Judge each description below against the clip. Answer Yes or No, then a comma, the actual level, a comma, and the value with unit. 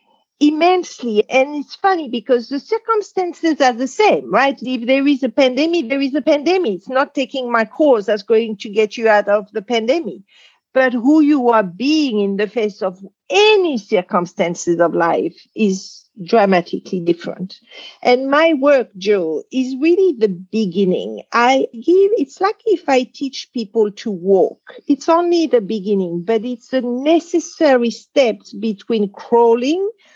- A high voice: Yes, very high, 250 Hz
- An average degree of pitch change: No, wide, 5.8 semitones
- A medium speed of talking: Yes, average, 155 wpm